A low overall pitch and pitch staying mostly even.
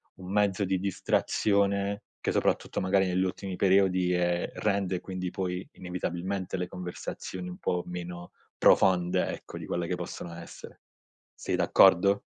Yes: very low, 90 Hz; narrow, 1.6 semitones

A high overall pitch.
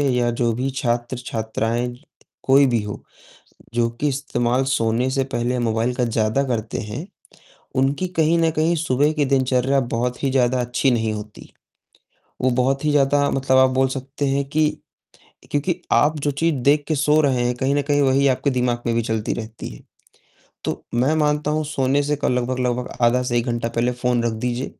No: low, 130 Hz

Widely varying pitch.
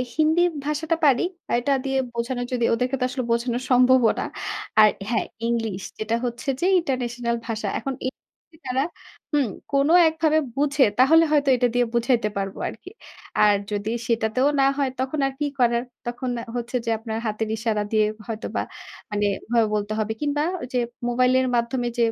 No: average, 3.1 semitones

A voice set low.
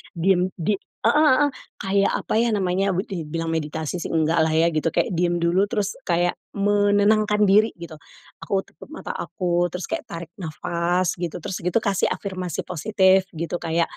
No: medium, 180 Hz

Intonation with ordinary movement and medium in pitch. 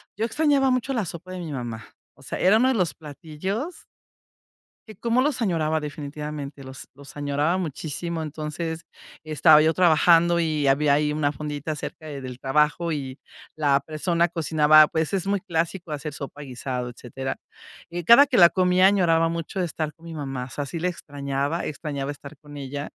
Yes: average, 3.3 semitones; medium, 155 Hz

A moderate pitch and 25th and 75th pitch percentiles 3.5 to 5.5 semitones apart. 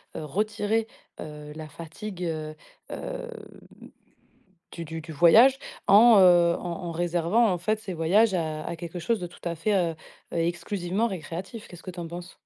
Yes: medium, 175 Hz; average, 3.9 semitones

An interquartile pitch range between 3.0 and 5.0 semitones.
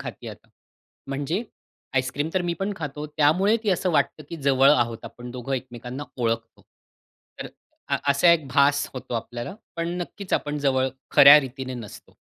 Yes: average, 3.9 semitones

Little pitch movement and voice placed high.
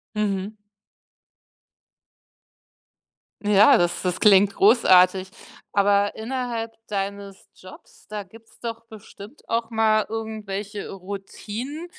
Yes: narrow, 2.3 semitones; high, 210 Hz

